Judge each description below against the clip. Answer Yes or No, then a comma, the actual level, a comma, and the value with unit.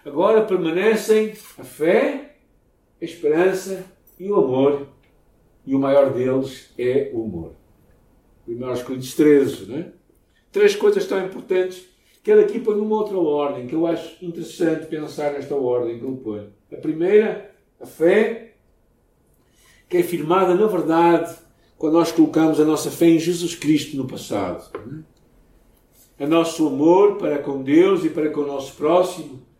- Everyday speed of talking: Yes, average, 150 wpm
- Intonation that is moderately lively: No, wide, 6.5 semitones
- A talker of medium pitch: Yes, medium, 165 Hz